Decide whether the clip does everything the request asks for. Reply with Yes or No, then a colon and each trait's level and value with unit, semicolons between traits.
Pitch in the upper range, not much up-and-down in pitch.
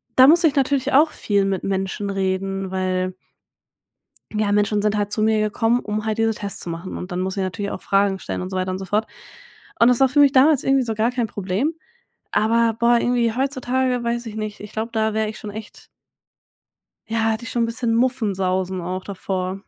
No: high, 215 Hz; average, 3.7 semitones